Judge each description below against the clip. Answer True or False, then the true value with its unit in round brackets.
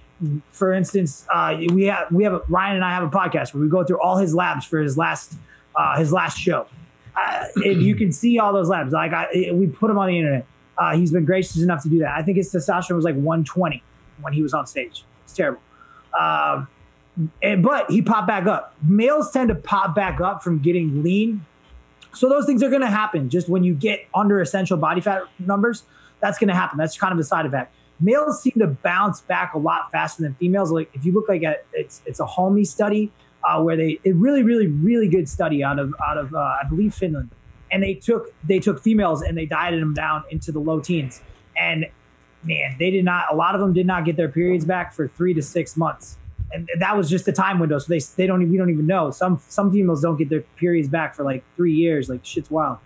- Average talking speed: False (240 wpm)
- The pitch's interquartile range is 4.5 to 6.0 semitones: False (3.8 semitones)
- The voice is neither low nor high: True (180 Hz)